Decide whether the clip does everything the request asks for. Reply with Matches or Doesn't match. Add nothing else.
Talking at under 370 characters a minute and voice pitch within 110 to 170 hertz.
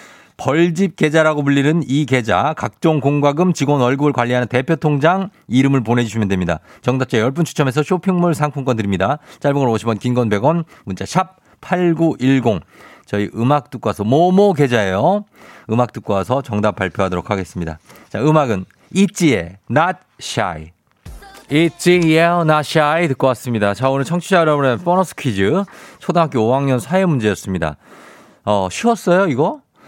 Matches